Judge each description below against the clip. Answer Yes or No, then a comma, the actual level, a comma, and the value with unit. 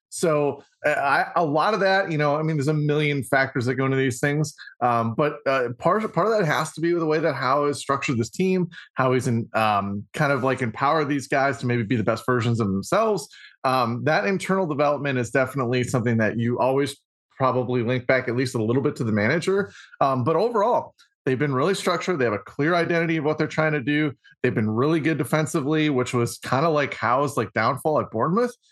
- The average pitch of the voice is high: No, medium, 140 Hz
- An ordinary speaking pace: No, fast, 235 wpm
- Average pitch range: Yes, average, 3.9 semitones